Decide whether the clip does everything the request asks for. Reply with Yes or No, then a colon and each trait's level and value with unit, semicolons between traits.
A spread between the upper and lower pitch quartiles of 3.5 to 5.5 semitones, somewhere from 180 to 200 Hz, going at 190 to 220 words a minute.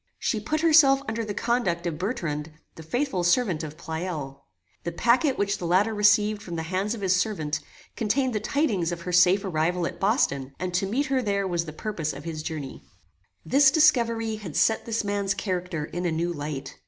Yes: average, 5.2 semitones; high, 190 Hz; average, 200 wpm